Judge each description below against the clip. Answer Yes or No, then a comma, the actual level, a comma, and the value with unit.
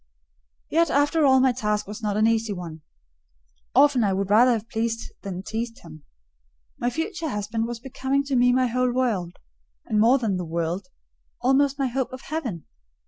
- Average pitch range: Yes, average, 4.1 semitones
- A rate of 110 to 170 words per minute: No, average, 180 wpm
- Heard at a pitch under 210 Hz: No, high, 235 Hz